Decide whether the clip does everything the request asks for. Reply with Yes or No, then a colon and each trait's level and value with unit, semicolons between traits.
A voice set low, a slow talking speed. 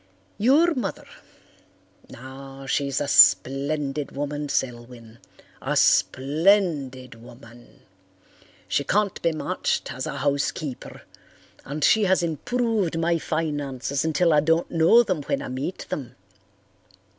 No: medium, 145 Hz; slow, 110 wpm